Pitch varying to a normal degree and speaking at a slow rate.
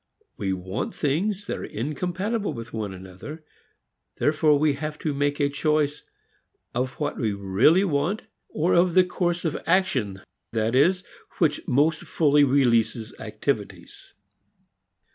No: wide, 6.1 semitones; slow, 130 wpm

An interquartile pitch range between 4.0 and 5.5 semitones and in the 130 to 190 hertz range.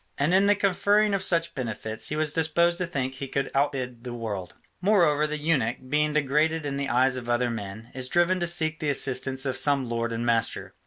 Yes: average, 4.8 semitones; medium, 140 Hz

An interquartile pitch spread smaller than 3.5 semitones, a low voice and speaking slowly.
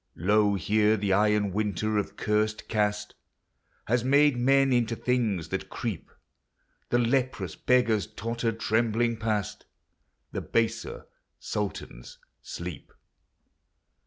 Yes: narrow, 2.4 semitones; low, 110 Hz; slow, 105 wpm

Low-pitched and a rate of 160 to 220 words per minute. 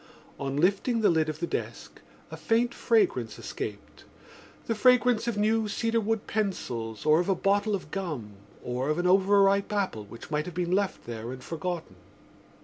No: high, 190 Hz; average, 165 wpm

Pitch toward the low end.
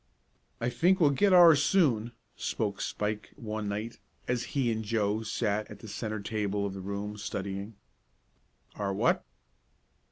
Yes: low, 110 Hz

